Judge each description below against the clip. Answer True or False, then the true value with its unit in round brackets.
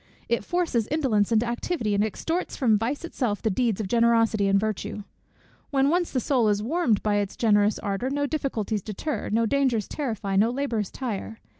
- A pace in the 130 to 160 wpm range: False (180 wpm)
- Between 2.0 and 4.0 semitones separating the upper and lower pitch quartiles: False (4.6 semitones)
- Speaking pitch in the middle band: False (230 Hz)